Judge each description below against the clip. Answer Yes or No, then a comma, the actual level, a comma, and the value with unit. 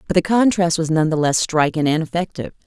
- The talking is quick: Yes, fast, 225 wpm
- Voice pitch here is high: No, medium, 165 Hz